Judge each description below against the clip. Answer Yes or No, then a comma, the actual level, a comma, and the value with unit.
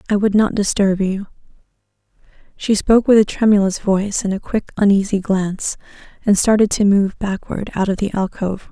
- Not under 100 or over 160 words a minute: No, average, 170 wpm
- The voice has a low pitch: No, high, 200 Hz